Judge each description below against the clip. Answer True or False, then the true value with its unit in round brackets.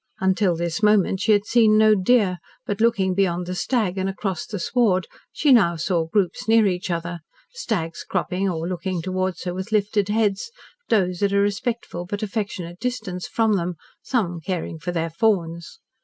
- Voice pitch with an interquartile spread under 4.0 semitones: True (3.3 semitones)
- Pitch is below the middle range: False (190 Hz)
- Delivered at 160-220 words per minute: True (175 wpm)